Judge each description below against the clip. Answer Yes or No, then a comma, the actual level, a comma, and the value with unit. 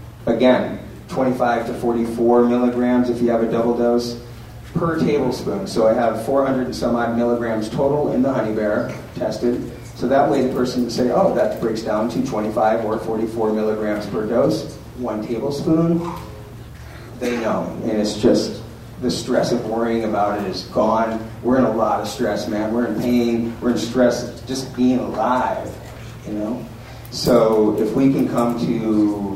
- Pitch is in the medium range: No, low, 120 Hz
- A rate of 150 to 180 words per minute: Yes, average, 170 wpm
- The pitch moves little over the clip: Yes, narrow, 1.8 semitones